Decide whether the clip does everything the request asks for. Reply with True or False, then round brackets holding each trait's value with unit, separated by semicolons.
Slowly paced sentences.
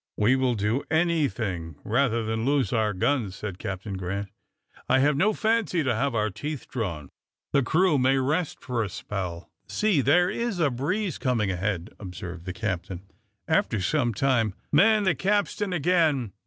False (165 wpm)